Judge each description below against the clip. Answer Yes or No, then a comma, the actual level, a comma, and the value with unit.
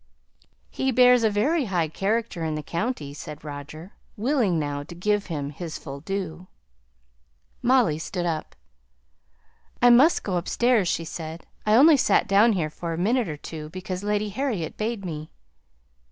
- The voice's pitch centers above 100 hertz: Yes, medium, 185 Hz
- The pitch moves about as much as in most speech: No, wide, 6.4 semitones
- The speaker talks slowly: No, average, 160 wpm